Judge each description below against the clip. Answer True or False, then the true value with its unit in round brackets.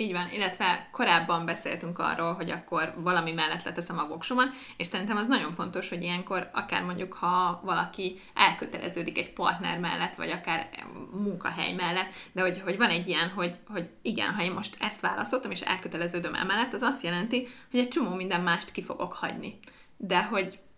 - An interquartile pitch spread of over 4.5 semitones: False (2.4 semitones)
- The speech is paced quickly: True (180 wpm)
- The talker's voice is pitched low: False (180 Hz)